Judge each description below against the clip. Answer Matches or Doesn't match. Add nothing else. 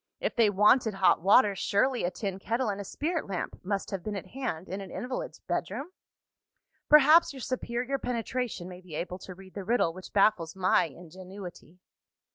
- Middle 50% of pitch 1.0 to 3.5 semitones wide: Doesn't match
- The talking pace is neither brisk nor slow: Matches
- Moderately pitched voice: Doesn't match